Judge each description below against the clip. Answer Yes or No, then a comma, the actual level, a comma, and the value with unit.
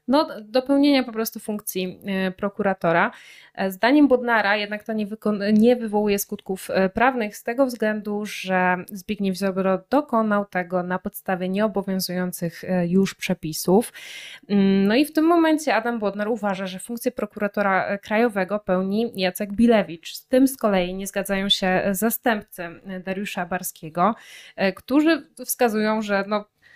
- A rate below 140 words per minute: Yes, average, 125 wpm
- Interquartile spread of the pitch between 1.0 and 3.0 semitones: No, average, 3.6 semitones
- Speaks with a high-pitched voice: Yes, high, 205 Hz